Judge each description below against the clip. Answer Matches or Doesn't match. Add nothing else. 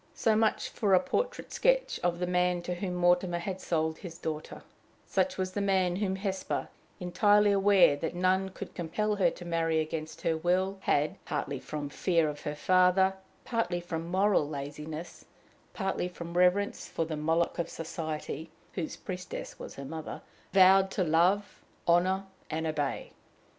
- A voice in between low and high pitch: Matches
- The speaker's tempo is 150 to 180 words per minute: Matches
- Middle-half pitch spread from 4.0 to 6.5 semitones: Doesn't match